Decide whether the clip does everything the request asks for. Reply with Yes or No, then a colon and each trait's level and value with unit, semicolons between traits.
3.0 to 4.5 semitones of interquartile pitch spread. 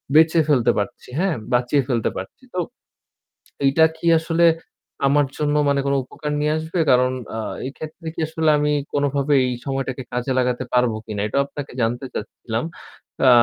Yes: average, 3.6 semitones